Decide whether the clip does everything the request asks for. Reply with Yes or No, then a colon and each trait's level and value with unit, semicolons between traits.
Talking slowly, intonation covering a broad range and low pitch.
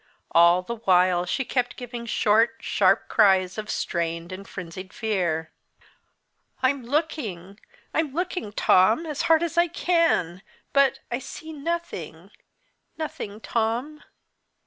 No: slow, 125 wpm; wide, 8.3 semitones; high, 225 Hz